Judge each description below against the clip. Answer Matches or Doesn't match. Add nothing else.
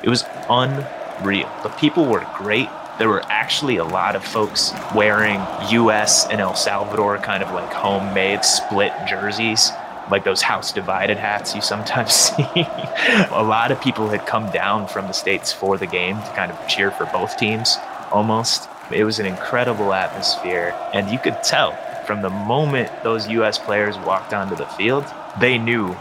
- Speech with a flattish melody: Matches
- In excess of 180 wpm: Doesn't match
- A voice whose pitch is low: Matches